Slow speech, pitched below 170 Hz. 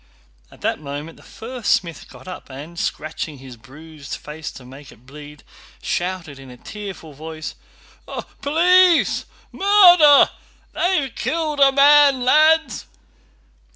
No: slow, 125 wpm; medium, 175 Hz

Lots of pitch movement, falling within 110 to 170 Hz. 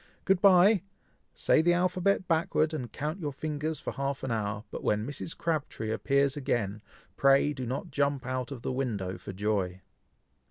Yes: wide, 5.7 semitones; medium, 140 Hz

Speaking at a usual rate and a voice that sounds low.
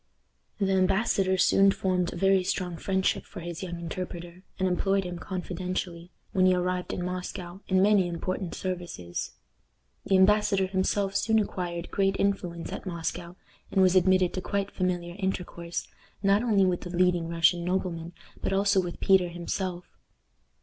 No: average, 155 wpm; medium, 185 Hz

